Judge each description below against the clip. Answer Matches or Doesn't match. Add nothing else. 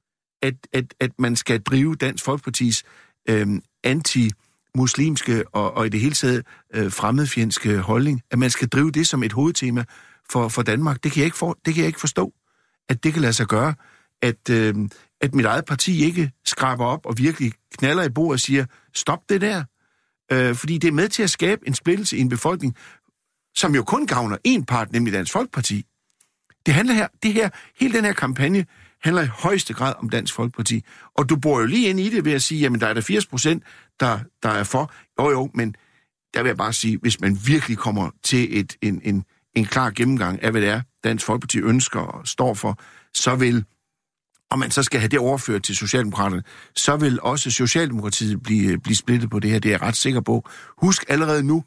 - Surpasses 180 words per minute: Matches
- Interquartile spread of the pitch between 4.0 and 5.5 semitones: Matches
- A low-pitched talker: Matches